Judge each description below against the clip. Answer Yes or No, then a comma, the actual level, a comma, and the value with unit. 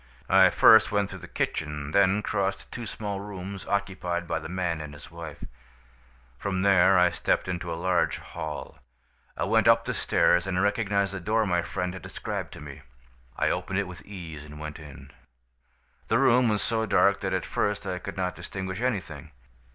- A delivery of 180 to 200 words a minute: Yes, average, 190 wpm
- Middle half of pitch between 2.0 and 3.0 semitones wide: Yes, narrow, 2.5 semitones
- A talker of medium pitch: No, very low, 95 Hz